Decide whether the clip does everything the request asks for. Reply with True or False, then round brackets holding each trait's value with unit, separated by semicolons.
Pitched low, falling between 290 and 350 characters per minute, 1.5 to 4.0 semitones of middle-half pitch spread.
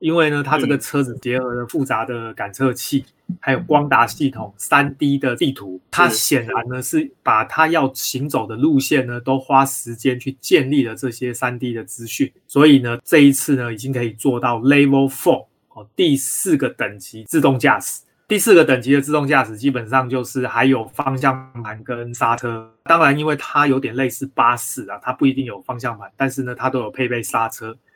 True (130 Hz; 305 characters per minute; 2.6 semitones)